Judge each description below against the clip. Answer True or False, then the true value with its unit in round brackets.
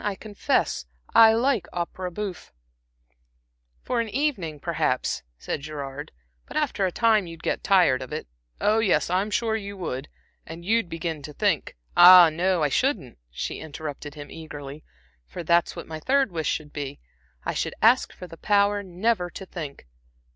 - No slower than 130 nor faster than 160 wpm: False (170 wpm)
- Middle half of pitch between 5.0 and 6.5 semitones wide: True (5.3 semitones)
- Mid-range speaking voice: True (175 Hz)